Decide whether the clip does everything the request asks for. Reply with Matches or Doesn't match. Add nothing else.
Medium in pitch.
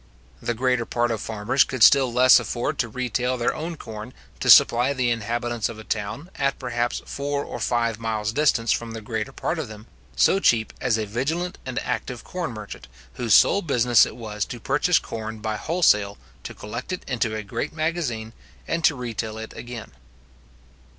Doesn't match